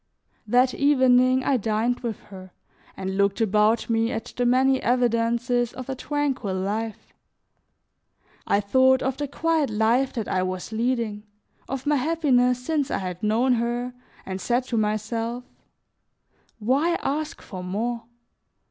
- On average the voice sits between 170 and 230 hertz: No, high, 240 Hz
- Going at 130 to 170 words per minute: Yes, average, 140 wpm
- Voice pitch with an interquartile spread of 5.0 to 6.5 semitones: No, average, 3.4 semitones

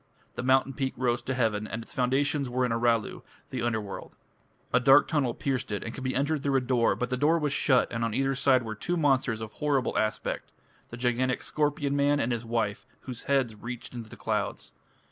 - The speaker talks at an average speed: No, fast, 215 wpm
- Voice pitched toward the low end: Yes, low, 125 Hz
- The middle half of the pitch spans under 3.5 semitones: Yes, average, 2.8 semitones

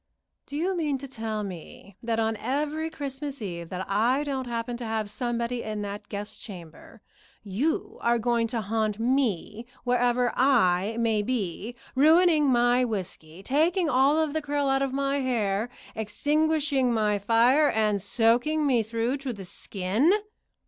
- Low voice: No, high, 240 Hz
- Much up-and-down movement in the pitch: No, average, 4.7 semitones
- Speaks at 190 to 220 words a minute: No, average, 155 wpm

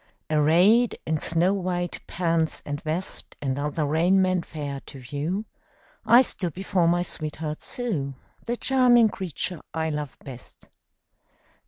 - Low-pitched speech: No, medium, 165 Hz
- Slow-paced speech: Yes, slow, 130 wpm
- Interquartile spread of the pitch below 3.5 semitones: No, average, 4.1 semitones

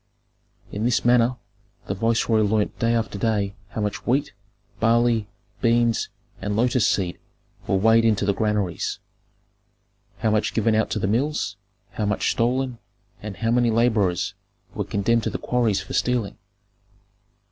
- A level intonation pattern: Yes, narrow, 2.3 semitones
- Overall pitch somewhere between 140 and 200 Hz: No, low, 110 Hz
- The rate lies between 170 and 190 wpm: No, average, 145 wpm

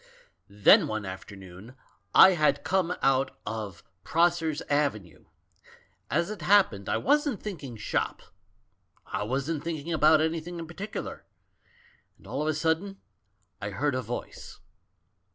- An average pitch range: No, wide, 7.4 semitones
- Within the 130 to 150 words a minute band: Yes, slow, 135 wpm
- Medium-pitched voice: Yes, medium, 150 Hz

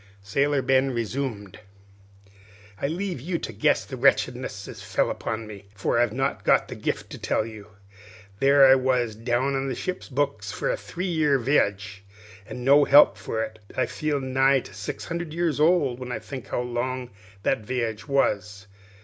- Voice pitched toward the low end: Yes, low, 130 Hz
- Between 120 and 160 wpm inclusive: No, average, 180 wpm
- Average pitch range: Yes, average, 4.1 semitones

